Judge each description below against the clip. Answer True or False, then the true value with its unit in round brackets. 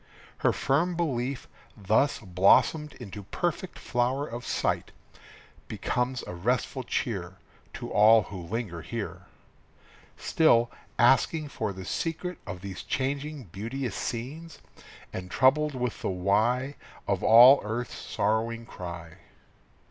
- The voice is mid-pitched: False (120 Hz)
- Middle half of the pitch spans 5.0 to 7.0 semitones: True (5.5 semitones)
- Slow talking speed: True (120 wpm)